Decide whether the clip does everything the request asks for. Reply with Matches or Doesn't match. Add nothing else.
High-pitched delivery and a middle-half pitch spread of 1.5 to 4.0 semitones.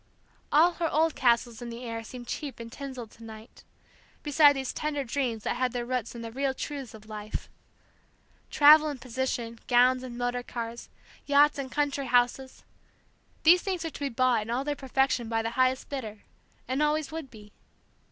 Matches